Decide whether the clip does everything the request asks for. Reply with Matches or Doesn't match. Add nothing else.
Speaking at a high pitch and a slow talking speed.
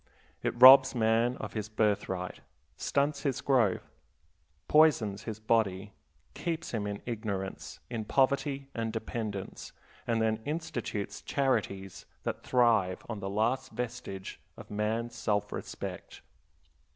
Doesn't match